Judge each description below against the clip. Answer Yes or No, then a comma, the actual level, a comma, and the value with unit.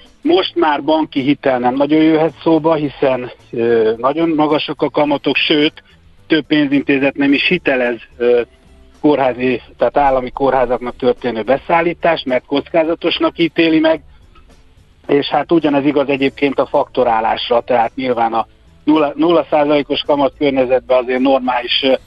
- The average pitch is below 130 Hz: No, medium, 140 Hz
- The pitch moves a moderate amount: Yes, average, 4.3 semitones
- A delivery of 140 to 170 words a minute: No, average, 130 wpm